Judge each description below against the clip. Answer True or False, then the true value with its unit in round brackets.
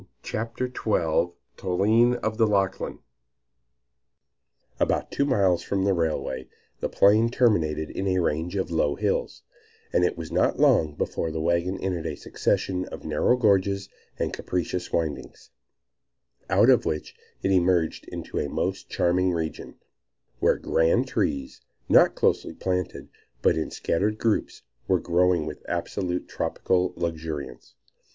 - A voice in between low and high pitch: False (90 Hz)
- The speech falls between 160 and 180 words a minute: False (135 wpm)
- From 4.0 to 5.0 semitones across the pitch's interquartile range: False (3.4 semitones)